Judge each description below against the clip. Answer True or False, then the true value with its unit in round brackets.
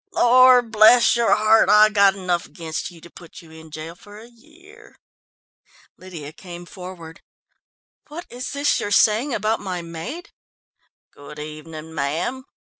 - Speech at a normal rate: True (145 wpm)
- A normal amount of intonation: False (6.4 semitones)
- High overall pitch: True (195 Hz)